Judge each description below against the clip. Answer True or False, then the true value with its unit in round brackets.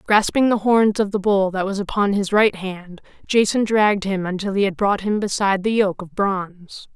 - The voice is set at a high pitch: True (200 Hz)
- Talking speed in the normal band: False (215 wpm)